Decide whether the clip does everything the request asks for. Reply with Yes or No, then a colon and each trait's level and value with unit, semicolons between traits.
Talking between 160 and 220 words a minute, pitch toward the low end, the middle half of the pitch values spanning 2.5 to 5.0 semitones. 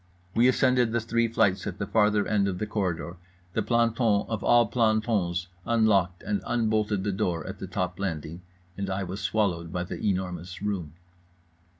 Yes: average, 175 wpm; low, 100 Hz; average, 3.6 semitones